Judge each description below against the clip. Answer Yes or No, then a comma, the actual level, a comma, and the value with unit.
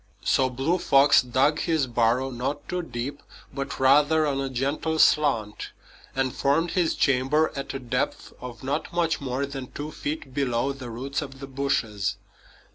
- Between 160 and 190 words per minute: Yes, average, 165 wpm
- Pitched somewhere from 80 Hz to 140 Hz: Yes, low, 135 Hz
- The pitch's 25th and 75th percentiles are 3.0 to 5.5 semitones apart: No, narrow, 2.5 semitones